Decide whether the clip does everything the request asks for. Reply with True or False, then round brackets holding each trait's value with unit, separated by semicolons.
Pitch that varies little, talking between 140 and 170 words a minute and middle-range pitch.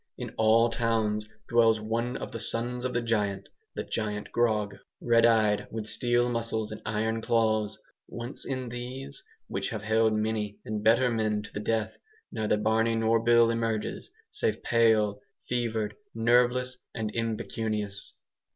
False (1.6 semitones; 150 wpm; 115 Hz)